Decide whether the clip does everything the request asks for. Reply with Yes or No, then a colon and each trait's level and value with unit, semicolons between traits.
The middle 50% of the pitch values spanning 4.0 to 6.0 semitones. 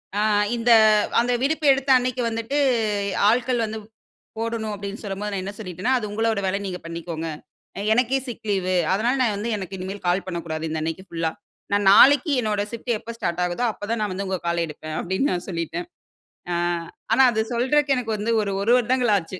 Yes: average, 4.5 semitones